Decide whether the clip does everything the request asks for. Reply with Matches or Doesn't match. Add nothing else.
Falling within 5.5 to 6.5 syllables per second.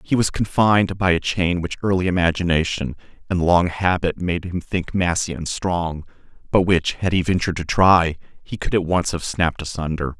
Doesn't match